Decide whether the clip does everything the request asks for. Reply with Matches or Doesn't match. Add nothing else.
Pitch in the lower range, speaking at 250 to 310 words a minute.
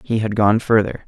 Doesn't match